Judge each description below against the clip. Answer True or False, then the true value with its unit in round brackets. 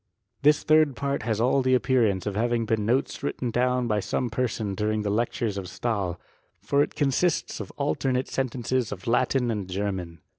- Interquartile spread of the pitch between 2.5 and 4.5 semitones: True (3.8 semitones)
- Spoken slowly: False (185 wpm)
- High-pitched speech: False (120 Hz)